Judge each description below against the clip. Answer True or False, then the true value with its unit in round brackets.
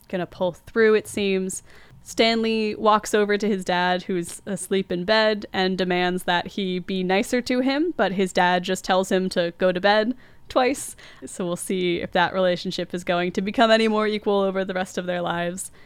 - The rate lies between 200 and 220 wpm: True (205 wpm)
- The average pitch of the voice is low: False (190 Hz)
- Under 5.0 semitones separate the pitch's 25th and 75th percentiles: True (2.9 semitones)